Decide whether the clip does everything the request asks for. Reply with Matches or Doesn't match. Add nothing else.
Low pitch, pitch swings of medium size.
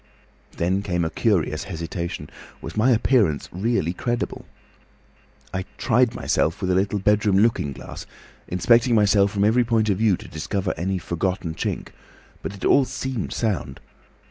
Matches